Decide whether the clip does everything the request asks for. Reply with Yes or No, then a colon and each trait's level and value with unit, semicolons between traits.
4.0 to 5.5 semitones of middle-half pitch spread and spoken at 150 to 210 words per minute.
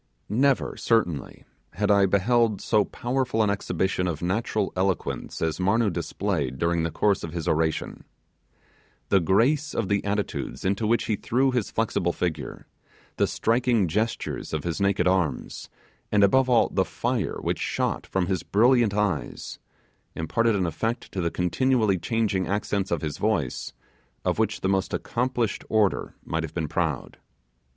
Yes: average, 4.4 semitones; average, 155 wpm